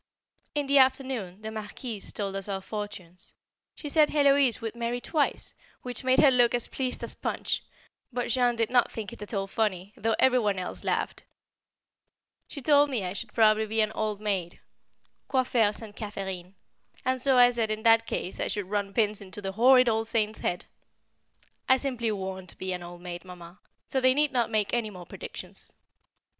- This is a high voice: Yes, high, 220 Hz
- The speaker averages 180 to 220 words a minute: Yes, average, 190 wpm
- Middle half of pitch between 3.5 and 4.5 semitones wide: Yes, average, 4.1 semitones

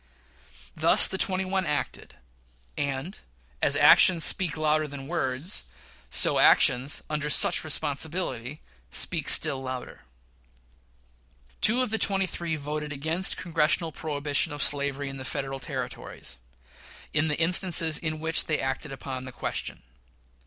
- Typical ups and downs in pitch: Yes, average, 3.2 semitones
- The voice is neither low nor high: Yes, medium, 150 Hz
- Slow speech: Yes, slow, 130 wpm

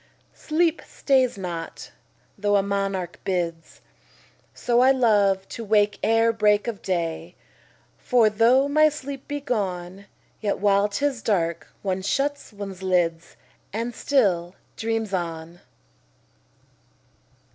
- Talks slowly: Yes, slow, 120 wpm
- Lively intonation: No, average, 4.7 semitones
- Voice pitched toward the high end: Yes, high, 205 Hz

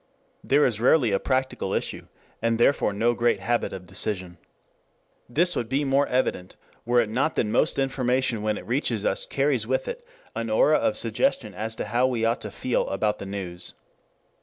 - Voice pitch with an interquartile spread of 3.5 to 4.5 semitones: Yes, average, 3.9 semitones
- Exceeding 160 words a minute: Yes, average, 185 wpm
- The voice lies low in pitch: Yes, low, 120 Hz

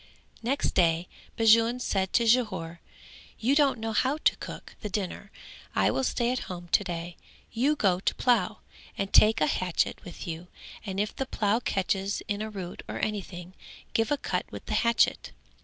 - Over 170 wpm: Yes, average, 180 wpm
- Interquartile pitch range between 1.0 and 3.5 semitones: No, average, 4.4 semitones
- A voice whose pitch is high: Yes, high, 210 Hz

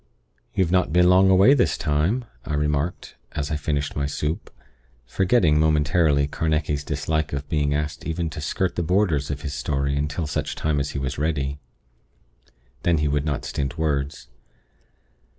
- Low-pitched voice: Yes, very low, 75 Hz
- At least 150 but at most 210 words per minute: Yes, average, 165 wpm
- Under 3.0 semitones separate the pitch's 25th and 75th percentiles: Yes, narrow, 2.5 semitones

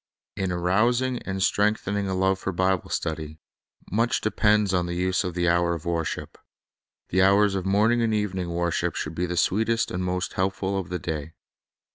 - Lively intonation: No, average, 2.8 semitones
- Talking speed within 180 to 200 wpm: Yes, average, 190 wpm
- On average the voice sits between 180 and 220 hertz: No, very low, 95 Hz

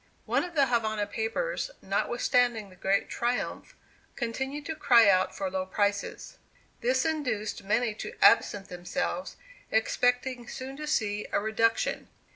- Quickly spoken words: No, slow, 135 wpm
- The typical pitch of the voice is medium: No, high, 230 Hz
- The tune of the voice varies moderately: Yes, average, 4.0 semitones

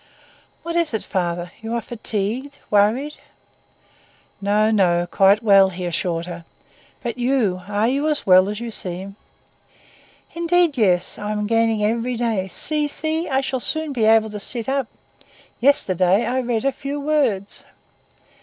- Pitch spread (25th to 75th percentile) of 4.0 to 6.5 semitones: Yes, wide, 5.6 semitones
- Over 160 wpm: No, average, 155 wpm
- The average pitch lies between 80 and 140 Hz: No, high, 225 Hz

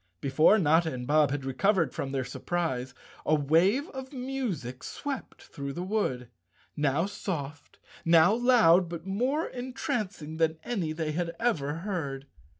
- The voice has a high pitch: No, medium, 165 Hz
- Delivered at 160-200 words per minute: No, average, 145 wpm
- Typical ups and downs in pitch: No, wide, 6.7 semitones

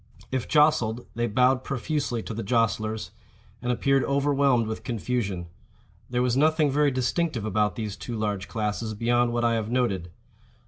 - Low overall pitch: Yes, low, 120 Hz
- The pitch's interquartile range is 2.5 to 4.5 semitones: Yes, average, 3.3 semitones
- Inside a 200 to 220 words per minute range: No, average, 150 wpm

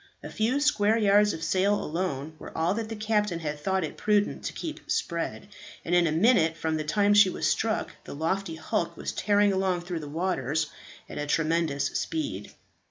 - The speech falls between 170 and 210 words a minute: Yes, average, 195 wpm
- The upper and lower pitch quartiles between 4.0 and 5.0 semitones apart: Yes, average, 4.5 semitones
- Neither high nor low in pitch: Yes, medium, 180 Hz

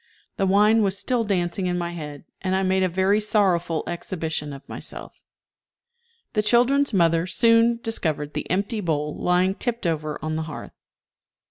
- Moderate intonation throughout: Yes, average, 4.4 semitones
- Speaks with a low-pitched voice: No, medium, 185 Hz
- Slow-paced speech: No, average, 160 wpm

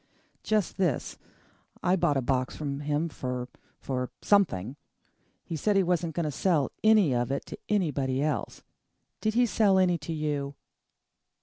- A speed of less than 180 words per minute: Yes, average, 155 wpm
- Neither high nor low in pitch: Yes, medium, 155 Hz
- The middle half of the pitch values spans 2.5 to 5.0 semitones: No, wide, 5.6 semitones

